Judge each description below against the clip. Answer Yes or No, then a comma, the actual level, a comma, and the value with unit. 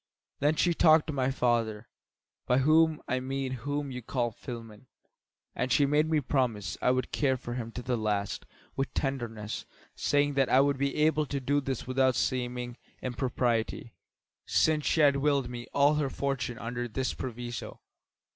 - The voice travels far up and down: No, average, 2.9 semitones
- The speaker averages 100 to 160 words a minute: No, average, 175 wpm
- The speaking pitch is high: No, low, 130 Hz